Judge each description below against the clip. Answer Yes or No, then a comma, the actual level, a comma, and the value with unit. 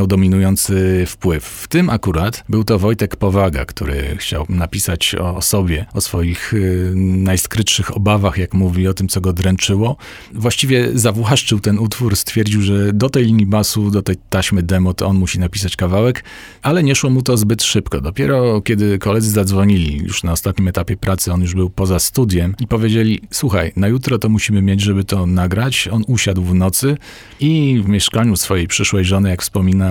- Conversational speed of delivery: No, fast, 180 wpm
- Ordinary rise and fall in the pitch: Yes, average, 3.1 semitones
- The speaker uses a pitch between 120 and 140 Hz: No, low, 100 Hz